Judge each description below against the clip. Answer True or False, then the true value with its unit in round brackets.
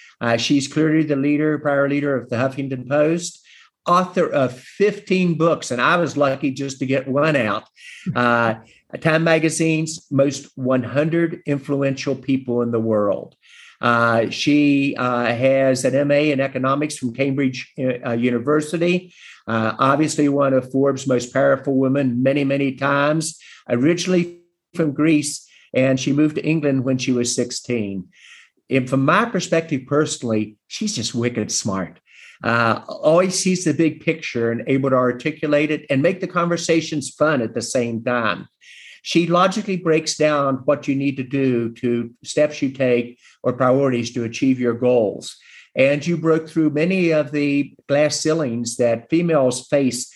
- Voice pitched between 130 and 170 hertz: True (140 Hz)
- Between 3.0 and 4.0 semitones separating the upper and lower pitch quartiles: True (3.7 semitones)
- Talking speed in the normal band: True (155 wpm)